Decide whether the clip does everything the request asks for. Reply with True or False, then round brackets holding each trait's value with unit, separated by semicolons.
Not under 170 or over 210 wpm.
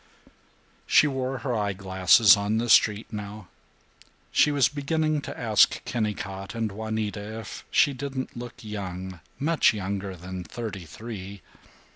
False (135 wpm)